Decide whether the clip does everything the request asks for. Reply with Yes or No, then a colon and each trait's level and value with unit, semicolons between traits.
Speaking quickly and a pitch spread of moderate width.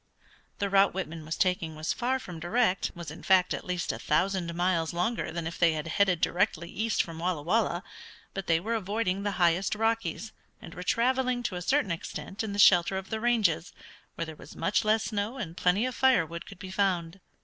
Yes: fast, 215 wpm; average, 4.3 semitones